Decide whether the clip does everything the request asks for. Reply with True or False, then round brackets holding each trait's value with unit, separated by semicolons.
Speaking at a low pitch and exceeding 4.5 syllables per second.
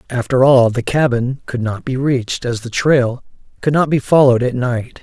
True (130 Hz; 5.0 syllables/s)